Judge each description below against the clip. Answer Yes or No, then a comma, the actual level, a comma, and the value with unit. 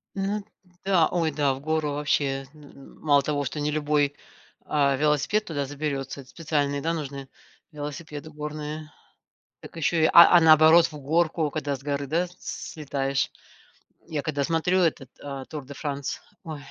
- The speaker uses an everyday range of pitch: No, narrow, 2.0 semitones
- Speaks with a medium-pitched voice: Yes, medium, 150 Hz